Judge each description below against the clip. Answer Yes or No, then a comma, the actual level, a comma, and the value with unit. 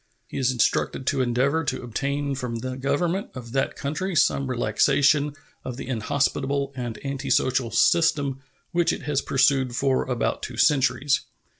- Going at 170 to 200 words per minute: No, average, 150 wpm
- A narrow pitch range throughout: Yes, narrow, 2.0 semitones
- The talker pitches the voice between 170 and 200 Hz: No, low, 135 Hz